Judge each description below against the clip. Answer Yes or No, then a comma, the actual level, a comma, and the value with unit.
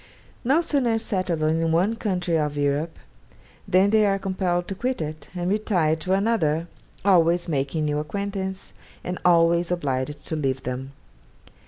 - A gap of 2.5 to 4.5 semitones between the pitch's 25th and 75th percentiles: Yes, average, 4.2 semitones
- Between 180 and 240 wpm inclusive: No, average, 150 wpm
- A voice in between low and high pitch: Yes, medium, 175 Hz